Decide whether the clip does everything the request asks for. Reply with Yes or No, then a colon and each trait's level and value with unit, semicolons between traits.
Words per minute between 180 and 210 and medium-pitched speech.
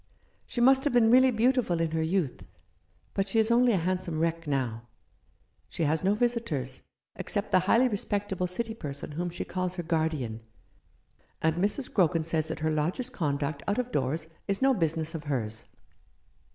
Yes: average, 195 wpm; medium, 175 Hz